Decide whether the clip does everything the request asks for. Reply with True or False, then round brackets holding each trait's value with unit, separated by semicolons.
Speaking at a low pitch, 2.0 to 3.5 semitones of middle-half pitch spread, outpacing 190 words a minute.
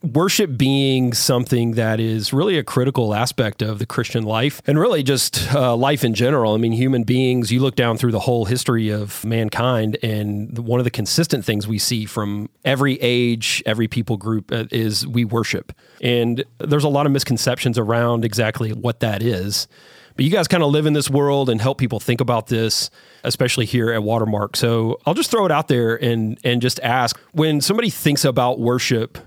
True (120 Hz; 2.9 semitones; 200 wpm)